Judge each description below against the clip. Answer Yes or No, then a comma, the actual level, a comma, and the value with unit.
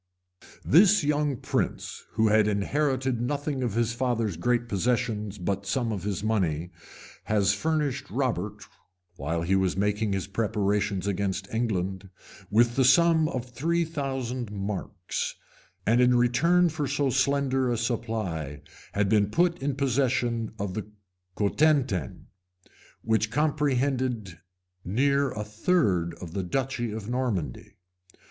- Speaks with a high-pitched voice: No, low, 115 Hz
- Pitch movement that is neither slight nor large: Yes, average, 4.9 semitones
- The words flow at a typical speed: No, slow, 130 wpm